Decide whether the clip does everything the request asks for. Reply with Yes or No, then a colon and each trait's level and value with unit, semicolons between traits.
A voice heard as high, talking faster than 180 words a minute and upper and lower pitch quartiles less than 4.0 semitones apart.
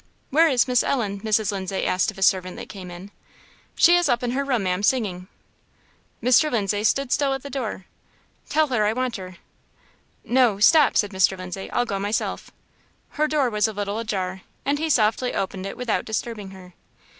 No: high, 215 Hz; average, 190 wpm; average, 4.9 semitones